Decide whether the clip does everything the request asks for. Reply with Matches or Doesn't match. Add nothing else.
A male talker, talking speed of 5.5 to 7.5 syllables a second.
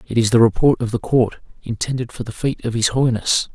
Matches